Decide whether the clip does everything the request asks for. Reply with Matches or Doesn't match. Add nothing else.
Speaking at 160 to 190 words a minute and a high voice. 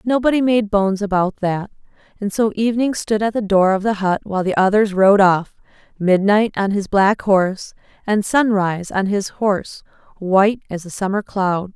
Matches